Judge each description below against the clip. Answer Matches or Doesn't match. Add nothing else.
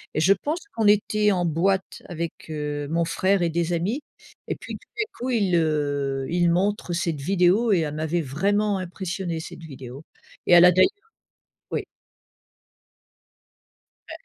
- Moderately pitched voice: Matches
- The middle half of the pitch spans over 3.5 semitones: Matches